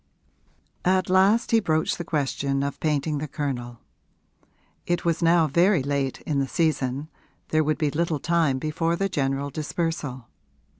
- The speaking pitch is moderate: Yes, medium, 155 Hz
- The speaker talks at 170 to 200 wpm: No, average, 155 wpm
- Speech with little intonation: No, average, 3.5 semitones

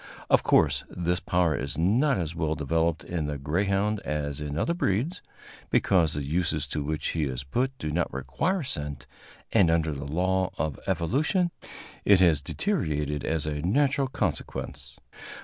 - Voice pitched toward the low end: Yes, very low, 80 Hz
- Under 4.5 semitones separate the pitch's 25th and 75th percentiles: No, average, 5.1 semitones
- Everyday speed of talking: Yes, average, 160 wpm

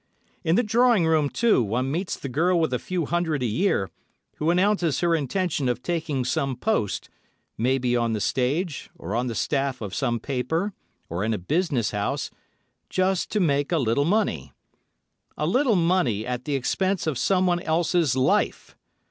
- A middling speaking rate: Yes, average, 170 wpm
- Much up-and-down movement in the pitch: Yes, wide, 6.2 semitones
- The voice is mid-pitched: Yes, medium, 150 Hz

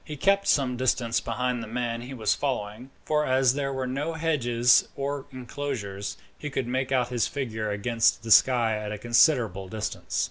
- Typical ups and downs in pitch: Yes, average, 3.2 semitones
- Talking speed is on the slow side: No, average, 180 wpm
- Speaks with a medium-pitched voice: No, low, 125 Hz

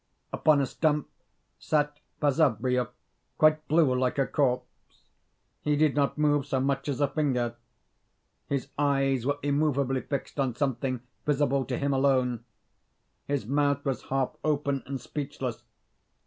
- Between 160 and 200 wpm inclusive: No, slow, 135 wpm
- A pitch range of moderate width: No, narrow, 2.2 semitones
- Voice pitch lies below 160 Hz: Yes, medium, 140 Hz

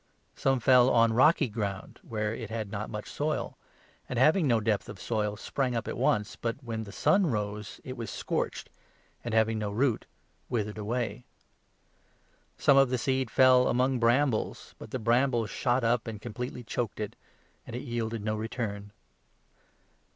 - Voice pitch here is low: Yes, low, 115 Hz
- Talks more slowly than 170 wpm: No, average, 175 wpm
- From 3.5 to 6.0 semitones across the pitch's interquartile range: No, average, 2.9 semitones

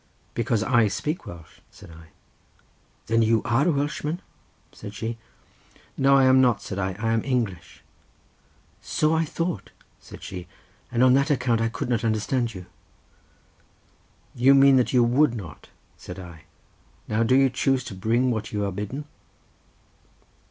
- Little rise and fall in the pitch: No, average, 4.2 semitones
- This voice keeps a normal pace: Yes, average, 160 wpm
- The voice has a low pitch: Yes, low, 120 Hz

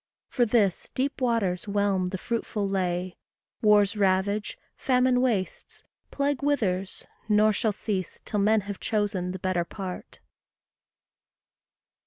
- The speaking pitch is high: Yes, high, 205 Hz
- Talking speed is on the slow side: Yes, slow, 120 wpm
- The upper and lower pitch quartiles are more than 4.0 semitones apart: No, average, 3.4 semitones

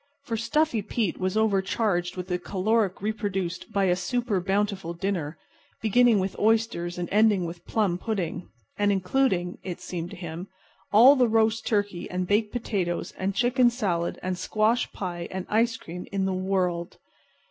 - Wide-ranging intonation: No, average, 3.6 semitones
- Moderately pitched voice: No, high, 195 Hz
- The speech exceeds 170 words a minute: No, average, 160 wpm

